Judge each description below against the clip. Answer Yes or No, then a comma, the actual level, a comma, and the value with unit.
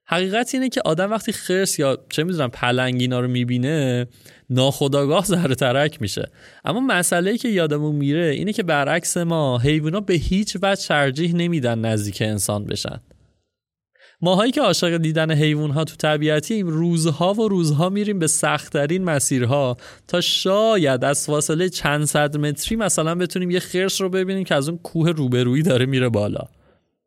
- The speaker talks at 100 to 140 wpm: No, fast, 155 wpm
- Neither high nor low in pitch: Yes, medium, 155 Hz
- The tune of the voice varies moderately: Yes, average, 4.6 semitones